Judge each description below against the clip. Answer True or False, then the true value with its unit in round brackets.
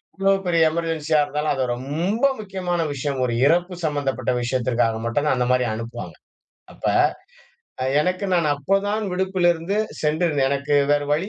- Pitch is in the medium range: True (150 Hz)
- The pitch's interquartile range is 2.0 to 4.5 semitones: False (5.0 semitones)